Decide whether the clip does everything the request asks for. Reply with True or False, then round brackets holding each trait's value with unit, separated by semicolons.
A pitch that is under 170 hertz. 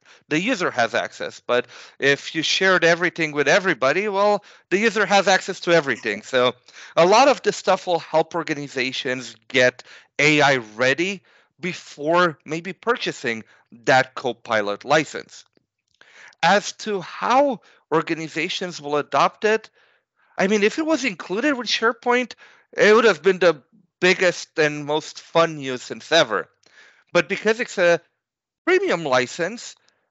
False (175 Hz)